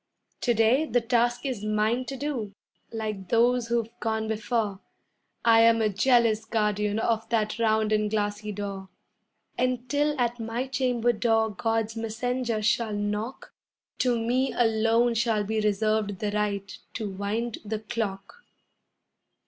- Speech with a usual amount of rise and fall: No, narrow, 2.1 semitones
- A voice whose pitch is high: Yes, high, 225 Hz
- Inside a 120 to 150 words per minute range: Yes, average, 140 wpm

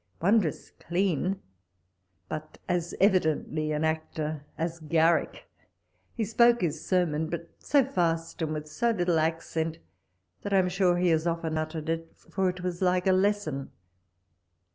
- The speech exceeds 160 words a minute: No, average, 145 wpm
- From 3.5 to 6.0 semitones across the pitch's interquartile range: No, average, 2.7 semitones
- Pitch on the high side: No, medium, 170 Hz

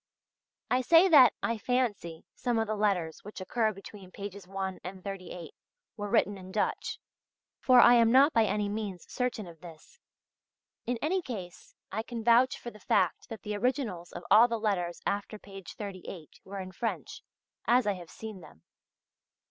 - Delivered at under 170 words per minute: No, average, 175 wpm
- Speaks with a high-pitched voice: Yes, high, 210 Hz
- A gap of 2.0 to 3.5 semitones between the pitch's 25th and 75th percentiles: No, average, 4.1 semitones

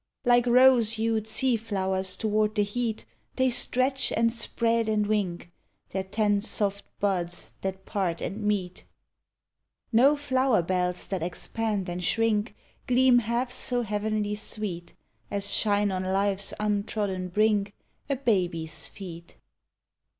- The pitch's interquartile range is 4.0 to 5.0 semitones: No, average, 3.2 semitones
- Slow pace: Yes, slow, 130 wpm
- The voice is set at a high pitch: Yes, high, 210 Hz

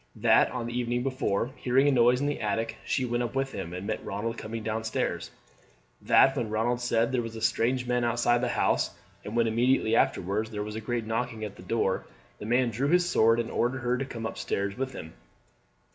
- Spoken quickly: Yes, fast, 220 wpm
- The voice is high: No, low, 115 Hz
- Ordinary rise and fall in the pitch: No, narrow, 2.0 semitones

